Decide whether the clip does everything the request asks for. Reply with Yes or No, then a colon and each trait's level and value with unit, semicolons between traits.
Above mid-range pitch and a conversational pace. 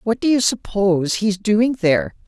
Yes: high, 210 Hz; average, 185 wpm